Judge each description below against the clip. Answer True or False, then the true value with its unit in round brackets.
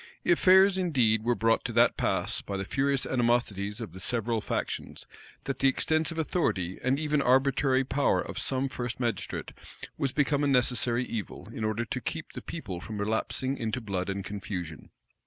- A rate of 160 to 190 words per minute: True (175 wpm)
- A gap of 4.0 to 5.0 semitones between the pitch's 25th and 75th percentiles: True (4.5 semitones)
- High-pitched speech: False (120 Hz)